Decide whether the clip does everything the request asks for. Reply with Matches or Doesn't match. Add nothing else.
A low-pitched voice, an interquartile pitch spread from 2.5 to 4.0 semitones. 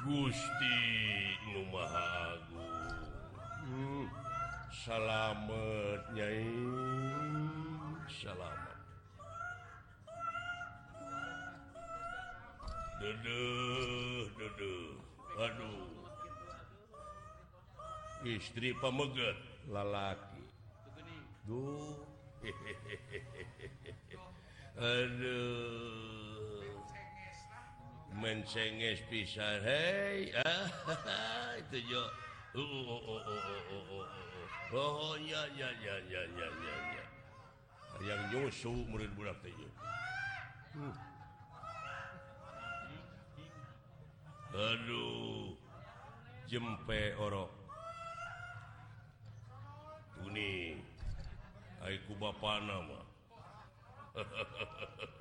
Doesn't match